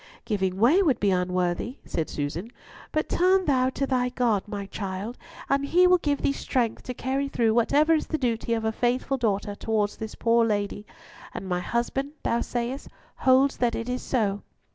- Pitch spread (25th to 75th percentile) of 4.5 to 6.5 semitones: Yes, average, 4.8 semitones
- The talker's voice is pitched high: Yes, high, 235 Hz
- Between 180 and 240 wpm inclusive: Yes, average, 185 wpm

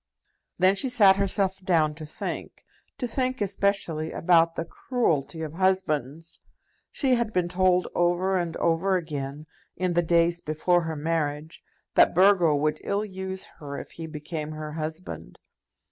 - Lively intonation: No, average, 3.4 semitones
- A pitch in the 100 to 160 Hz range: No, medium, 170 Hz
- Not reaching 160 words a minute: Yes, average, 150 wpm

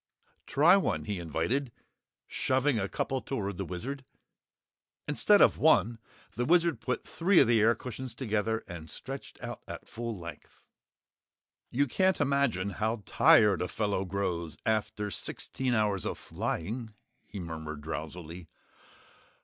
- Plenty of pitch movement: Yes, wide, 6.4 semitones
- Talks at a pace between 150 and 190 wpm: No, slow, 135 wpm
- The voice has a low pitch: Yes, low, 110 Hz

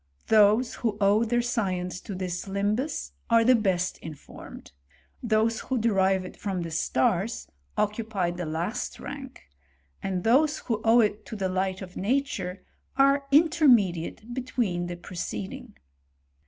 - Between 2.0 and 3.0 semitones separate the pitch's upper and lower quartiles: No, average, 4.7 semitones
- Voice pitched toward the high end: Yes, high, 210 Hz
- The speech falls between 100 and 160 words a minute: Yes, average, 140 wpm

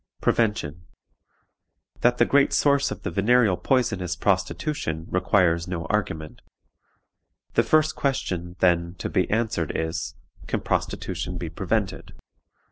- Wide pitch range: Yes, wide, 5.7 semitones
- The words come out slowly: Yes, slow, 125 wpm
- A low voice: Yes, very low, 90 Hz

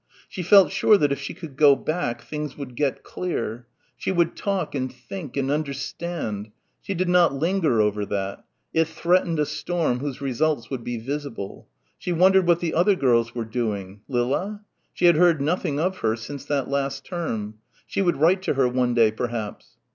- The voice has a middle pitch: Yes, medium, 145 Hz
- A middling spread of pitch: No, wide, 6.0 semitones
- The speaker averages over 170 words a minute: Yes, average, 185 wpm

